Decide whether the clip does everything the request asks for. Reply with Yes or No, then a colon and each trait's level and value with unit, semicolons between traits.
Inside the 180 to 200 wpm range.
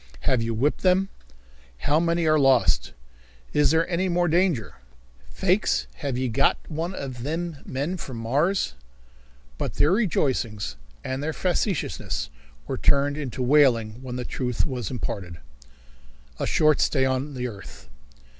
No: average, 145 wpm